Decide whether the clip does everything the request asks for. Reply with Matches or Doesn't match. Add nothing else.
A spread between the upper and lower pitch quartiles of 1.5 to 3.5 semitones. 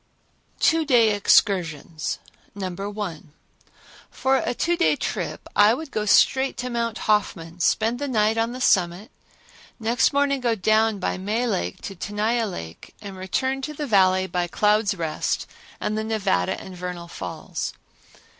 Doesn't match